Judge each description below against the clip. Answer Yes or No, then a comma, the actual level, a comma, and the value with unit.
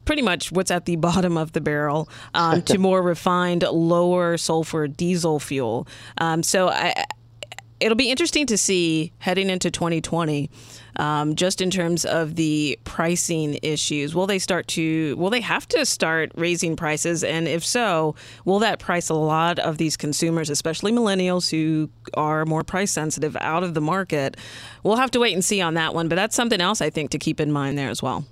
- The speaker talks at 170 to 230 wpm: Yes, average, 195 wpm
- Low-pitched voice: No, medium, 165 Hz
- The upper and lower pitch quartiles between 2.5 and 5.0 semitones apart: Yes, average, 3.1 semitones